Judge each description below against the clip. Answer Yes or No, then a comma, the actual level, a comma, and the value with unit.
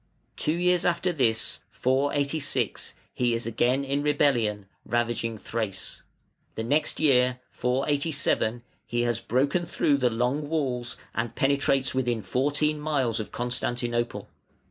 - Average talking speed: No, slow, 120 wpm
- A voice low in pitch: Yes, low, 130 Hz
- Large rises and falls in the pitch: No, average, 3.4 semitones